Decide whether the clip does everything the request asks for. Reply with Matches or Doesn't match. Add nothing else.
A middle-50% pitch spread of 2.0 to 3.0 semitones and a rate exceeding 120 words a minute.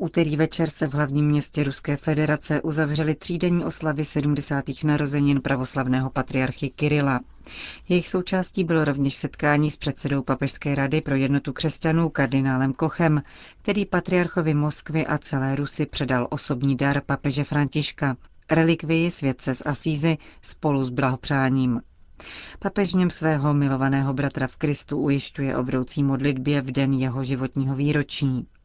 Matches